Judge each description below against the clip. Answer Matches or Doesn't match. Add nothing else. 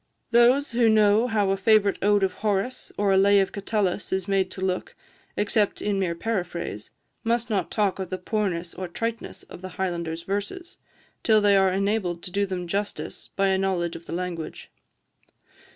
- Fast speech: Doesn't match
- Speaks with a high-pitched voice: Matches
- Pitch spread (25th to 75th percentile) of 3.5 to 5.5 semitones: Doesn't match